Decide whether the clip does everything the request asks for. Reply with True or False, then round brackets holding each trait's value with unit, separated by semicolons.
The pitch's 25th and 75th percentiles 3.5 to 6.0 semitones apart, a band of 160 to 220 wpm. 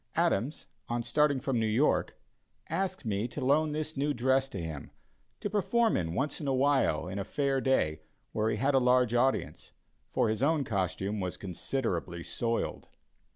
True (5.6 semitones; 175 wpm)